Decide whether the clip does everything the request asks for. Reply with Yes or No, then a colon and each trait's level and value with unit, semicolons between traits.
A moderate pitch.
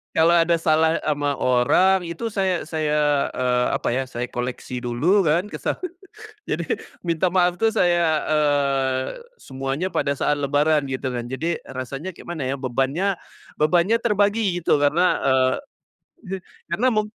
Yes: medium, 155 Hz